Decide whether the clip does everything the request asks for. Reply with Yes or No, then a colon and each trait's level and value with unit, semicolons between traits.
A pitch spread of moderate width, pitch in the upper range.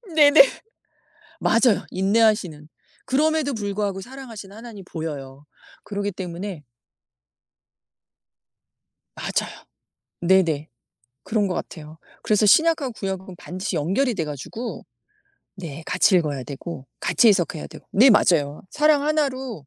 No: wide, 6.3 semitones; high, 195 Hz